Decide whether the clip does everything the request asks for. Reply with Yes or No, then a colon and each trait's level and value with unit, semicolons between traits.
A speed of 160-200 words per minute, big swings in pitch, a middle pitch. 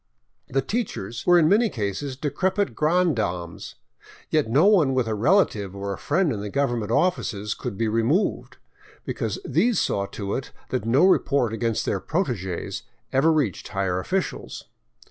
No: average, 165 wpm; wide, 8.5 semitones; low, 130 Hz